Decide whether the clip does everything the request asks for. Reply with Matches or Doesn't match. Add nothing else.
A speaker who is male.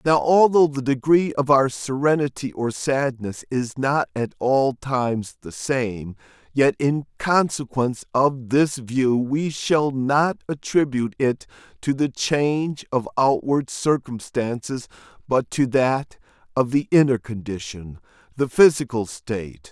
Matches